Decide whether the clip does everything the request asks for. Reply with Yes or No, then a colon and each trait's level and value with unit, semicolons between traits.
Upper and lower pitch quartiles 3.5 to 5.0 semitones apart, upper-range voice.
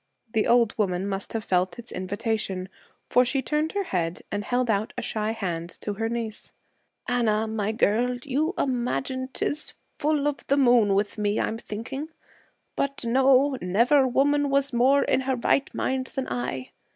Yes: average, 4.5 semitones; high, 235 Hz